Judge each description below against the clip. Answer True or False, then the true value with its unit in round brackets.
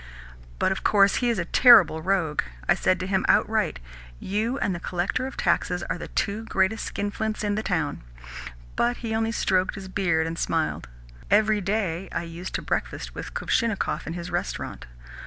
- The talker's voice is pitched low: False (195 Hz)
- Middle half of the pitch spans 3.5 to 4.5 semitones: True (3.8 semitones)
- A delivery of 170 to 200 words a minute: True (180 wpm)